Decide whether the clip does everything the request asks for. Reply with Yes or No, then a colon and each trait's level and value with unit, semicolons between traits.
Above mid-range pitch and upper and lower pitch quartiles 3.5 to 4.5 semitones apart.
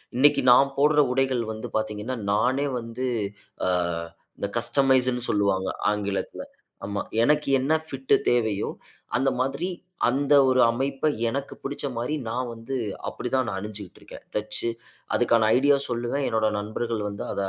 No: low, 120 Hz; average, 3.8 semitones